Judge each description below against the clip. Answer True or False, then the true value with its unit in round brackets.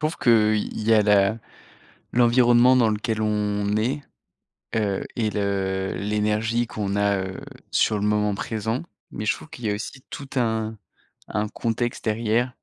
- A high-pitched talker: False (110 Hz)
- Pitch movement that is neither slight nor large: False (2.2 semitones)